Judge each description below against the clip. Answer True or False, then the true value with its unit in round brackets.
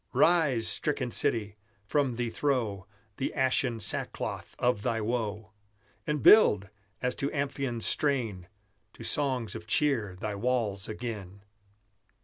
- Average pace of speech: False (125 wpm)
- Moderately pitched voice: False (120 Hz)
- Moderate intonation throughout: True (4.3 semitones)